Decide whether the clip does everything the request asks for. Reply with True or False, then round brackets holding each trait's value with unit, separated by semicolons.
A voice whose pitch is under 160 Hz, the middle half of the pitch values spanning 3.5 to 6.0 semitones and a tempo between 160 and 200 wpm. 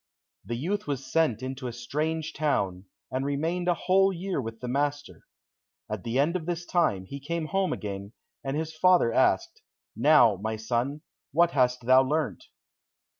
True (140 Hz; 5.6 semitones; 170 wpm)